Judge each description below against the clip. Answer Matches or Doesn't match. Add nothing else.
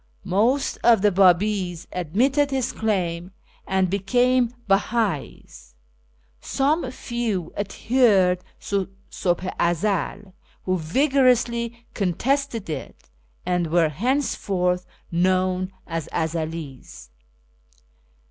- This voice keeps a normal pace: Doesn't match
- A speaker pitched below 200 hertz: Matches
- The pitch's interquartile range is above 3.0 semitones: Matches